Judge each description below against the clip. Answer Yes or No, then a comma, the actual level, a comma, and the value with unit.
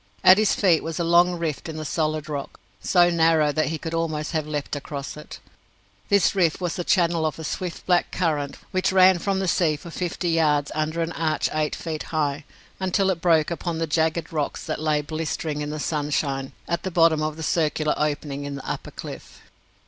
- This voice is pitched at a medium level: Yes, medium, 160 Hz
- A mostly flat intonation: Yes, narrow, 2.2 semitones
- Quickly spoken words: Yes, fast, 210 wpm